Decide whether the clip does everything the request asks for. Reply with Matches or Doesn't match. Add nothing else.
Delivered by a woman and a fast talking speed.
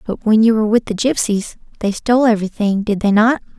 Matches